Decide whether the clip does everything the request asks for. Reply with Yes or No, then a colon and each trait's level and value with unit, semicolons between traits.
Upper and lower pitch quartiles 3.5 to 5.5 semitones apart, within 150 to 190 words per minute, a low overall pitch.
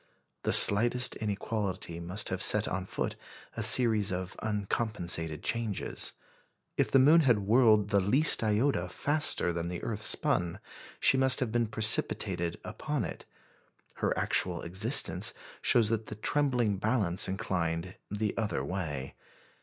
No: average, 4.2 semitones; average, 140 wpm; low, 105 Hz